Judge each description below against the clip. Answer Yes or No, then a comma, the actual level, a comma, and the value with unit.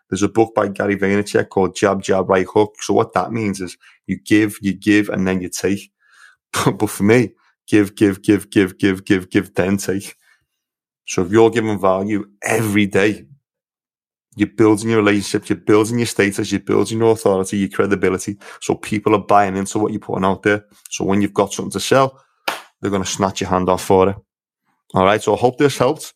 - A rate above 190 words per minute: Yes, fast, 205 wpm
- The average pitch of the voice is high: No, low, 100 Hz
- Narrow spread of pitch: Yes, narrow, 1.8 semitones